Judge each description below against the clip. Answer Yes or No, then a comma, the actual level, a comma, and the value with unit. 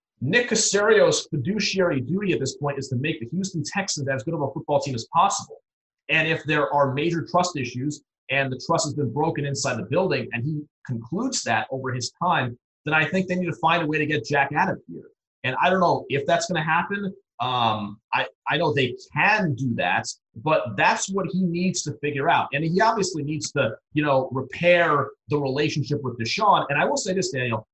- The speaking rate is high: Yes, fast, 220 wpm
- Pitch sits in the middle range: Yes, medium, 150 Hz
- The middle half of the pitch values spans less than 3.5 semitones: No, average, 4.5 semitones